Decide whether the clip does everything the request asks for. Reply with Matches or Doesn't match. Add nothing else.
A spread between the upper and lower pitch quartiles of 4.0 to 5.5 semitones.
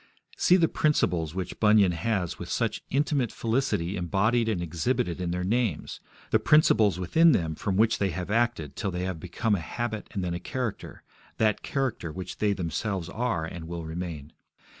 Matches